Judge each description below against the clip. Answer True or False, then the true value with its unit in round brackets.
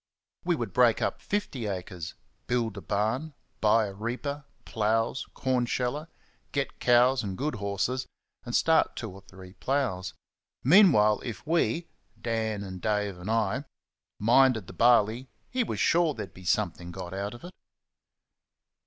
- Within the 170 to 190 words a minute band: False (145 wpm)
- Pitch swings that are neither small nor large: True (4.7 semitones)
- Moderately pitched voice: False (115 Hz)